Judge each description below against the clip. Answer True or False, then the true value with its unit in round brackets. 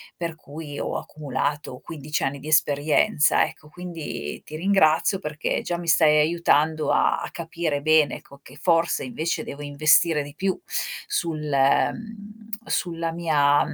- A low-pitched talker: False (155 Hz)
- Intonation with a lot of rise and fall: False (2.6 semitones)